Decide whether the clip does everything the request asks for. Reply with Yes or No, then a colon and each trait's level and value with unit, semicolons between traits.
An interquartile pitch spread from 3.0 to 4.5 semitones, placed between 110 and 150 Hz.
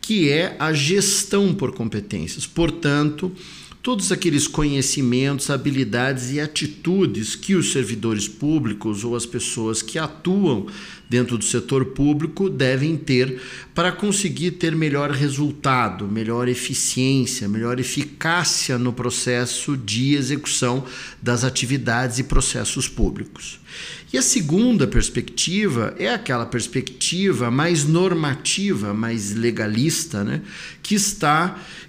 No: average, 5.2 semitones; medium, 140 Hz